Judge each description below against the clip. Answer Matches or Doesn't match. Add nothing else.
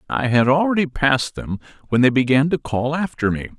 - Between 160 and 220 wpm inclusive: Matches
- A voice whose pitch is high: Doesn't match